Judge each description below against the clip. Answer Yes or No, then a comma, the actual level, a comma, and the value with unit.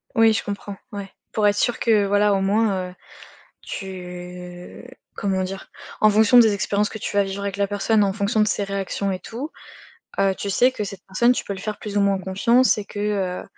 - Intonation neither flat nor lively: No, narrow, 1.6 semitones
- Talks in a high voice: Yes, high, 200 Hz